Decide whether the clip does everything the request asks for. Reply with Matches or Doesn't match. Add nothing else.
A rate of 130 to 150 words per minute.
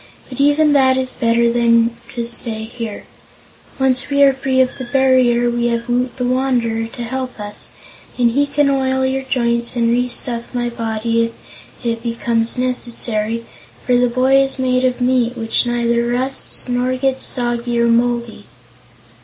Doesn't match